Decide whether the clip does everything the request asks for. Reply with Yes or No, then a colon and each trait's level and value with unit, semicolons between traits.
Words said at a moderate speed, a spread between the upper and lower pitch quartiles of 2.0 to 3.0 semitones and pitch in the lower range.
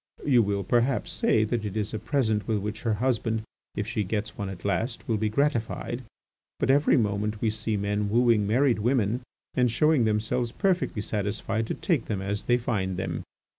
Yes: average, 190 wpm; average, 2.7 semitones; low, 110 Hz